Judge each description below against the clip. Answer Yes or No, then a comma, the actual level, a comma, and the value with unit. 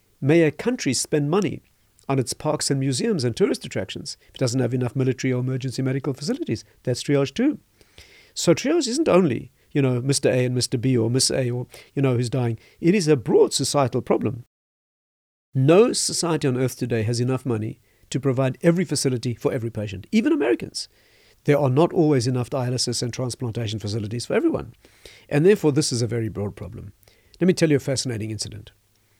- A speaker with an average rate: Yes, average, 195 wpm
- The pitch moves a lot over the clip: No, average, 3.6 semitones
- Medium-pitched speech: No, low, 130 Hz